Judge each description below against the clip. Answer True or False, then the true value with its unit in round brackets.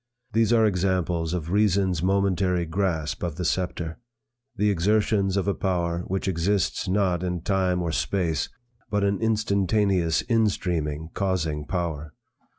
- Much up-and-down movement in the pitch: False (2.8 semitones)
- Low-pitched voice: True (95 Hz)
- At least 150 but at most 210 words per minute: False (140 wpm)